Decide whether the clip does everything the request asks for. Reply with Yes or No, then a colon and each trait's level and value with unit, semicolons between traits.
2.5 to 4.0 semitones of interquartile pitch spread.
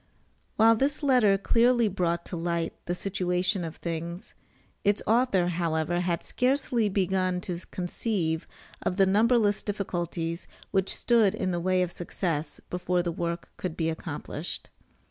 Yes: average, 3.2 semitones